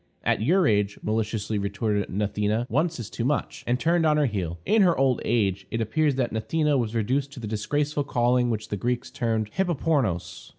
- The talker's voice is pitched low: Yes, low, 120 Hz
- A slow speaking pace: No, average, 195 wpm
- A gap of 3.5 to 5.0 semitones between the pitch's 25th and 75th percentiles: No, wide, 5.5 semitones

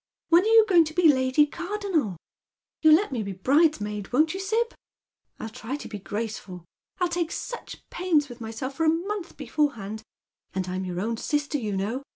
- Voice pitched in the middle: No, very high, 285 Hz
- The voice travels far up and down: Yes, wide, 7.9 semitones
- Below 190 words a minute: No, average, 195 wpm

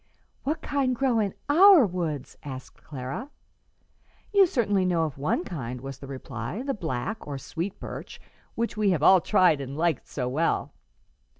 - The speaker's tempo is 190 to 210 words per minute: No, average, 165 wpm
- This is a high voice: No, medium, 175 Hz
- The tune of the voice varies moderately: No, wide, 8.5 semitones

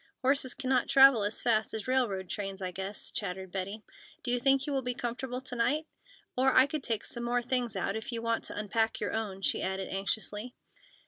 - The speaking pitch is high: Yes, high, 230 Hz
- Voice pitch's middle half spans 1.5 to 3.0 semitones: No, average, 4.2 semitones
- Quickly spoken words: Yes, fast, 210 wpm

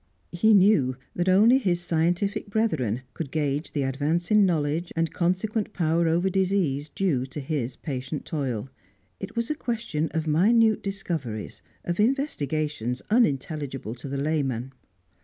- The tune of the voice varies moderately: No, wide, 5.9 semitones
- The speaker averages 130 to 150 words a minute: Yes, average, 140 wpm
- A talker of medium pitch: Yes, medium, 160 Hz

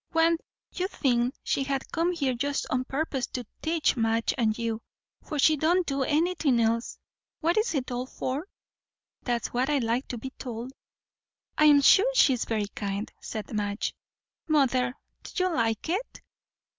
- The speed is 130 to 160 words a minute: Yes, average, 155 wpm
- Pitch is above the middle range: Yes, very high, 265 Hz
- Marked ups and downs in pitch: No, average, 5.0 semitones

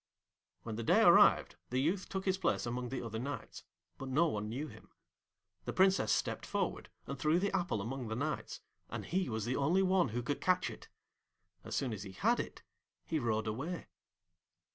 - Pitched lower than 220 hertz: Yes, low, 135 Hz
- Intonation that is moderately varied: No, wide, 7.4 semitones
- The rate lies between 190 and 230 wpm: Yes, average, 195 wpm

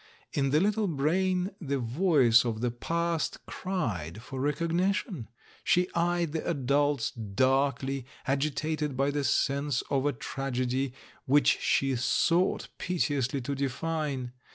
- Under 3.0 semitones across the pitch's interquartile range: No, average, 4.3 semitones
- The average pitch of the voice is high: No, medium, 140 Hz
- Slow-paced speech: Yes, slow, 130 wpm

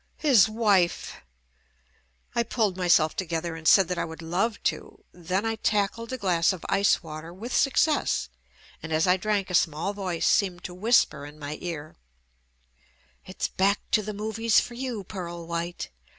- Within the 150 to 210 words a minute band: Yes, average, 165 wpm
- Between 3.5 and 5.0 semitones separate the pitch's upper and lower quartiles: Yes, average, 4.2 semitones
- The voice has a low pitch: No, medium, 185 Hz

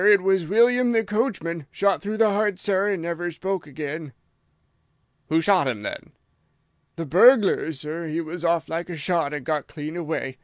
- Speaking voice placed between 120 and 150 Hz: No, medium, 170 Hz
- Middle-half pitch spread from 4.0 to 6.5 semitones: Yes, average, 4.3 semitones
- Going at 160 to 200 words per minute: Yes, average, 180 wpm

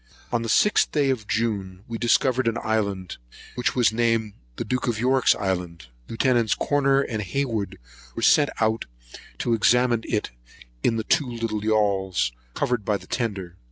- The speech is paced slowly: No, average, 155 wpm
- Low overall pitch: Yes, low, 115 Hz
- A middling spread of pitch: Yes, average, 3.2 semitones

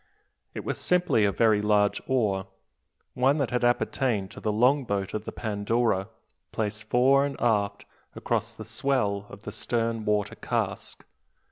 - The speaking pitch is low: Yes, low, 110 Hz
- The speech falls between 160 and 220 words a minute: No, average, 150 wpm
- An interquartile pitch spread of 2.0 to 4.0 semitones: Yes, average, 3.2 semitones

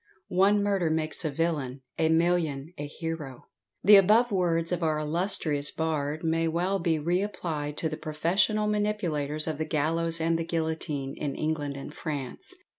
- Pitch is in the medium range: Yes, medium, 160 Hz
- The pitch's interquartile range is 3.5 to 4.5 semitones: No, average, 2.7 semitones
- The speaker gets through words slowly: No, average, 165 wpm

